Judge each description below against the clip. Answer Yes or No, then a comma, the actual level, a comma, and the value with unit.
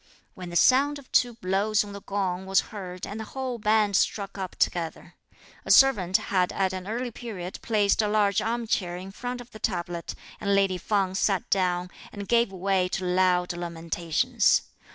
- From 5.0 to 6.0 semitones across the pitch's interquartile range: No, average, 3.0 semitones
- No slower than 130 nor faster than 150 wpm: No, average, 180 wpm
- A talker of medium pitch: No, high, 195 Hz